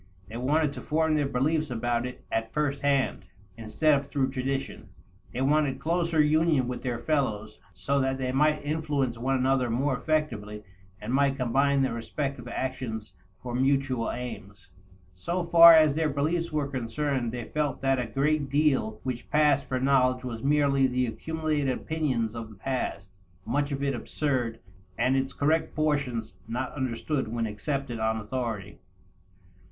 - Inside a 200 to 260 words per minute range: No, average, 160 wpm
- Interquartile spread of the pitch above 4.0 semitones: No, average, 3.7 semitones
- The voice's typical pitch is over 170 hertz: No, low, 135 Hz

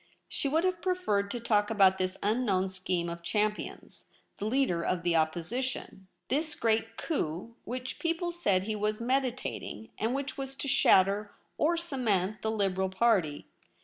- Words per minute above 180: No, average, 160 wpm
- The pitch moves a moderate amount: No, wide, 5.8 semitones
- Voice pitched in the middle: No, high, 215 Hz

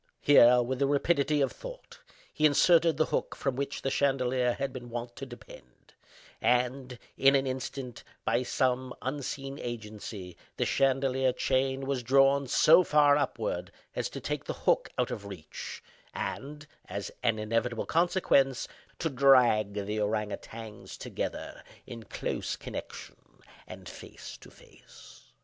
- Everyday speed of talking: Yes, average, 145 wpm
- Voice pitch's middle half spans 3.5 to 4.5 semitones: No, average, 2.7 semitones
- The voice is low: Yes, low, 130 Hz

